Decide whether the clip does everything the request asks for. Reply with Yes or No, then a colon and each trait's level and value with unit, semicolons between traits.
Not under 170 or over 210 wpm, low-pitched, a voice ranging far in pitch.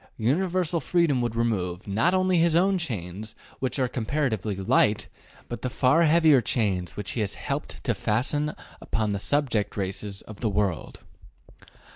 No: average, 155 wpm; low, 120 Hz; wide, 6.7 semitones